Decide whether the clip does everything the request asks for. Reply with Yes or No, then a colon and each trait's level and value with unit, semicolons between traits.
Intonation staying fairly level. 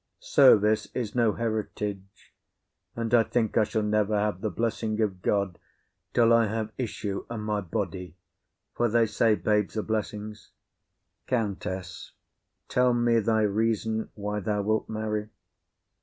Yes: narrow, 1.6 semitones